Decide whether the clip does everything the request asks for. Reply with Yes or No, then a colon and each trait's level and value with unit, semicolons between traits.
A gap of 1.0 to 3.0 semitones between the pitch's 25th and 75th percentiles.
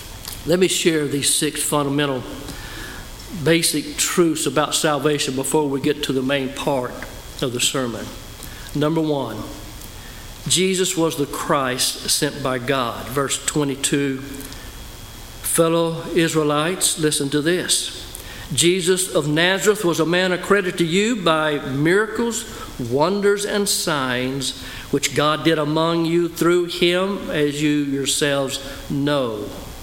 No: average, 3.7 semitones